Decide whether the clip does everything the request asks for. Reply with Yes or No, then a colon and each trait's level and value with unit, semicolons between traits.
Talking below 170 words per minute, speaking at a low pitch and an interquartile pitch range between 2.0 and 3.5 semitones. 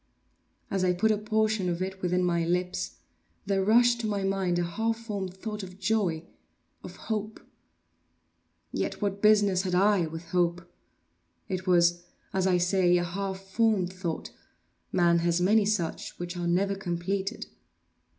No: average, 150 wpm; high, 190 Hz; narrow, 2.6 semitones